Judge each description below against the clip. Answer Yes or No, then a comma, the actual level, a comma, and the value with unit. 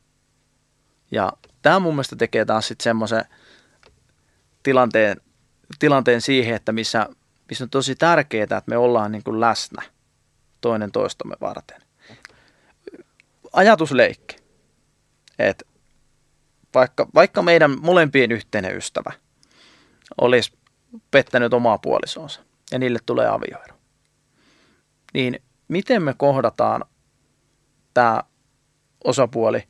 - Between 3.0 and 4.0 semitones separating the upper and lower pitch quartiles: Yes, average, 3.5 semitones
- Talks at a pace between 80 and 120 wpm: Yes, slow, 95 wpm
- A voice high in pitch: No, low, 125 Hz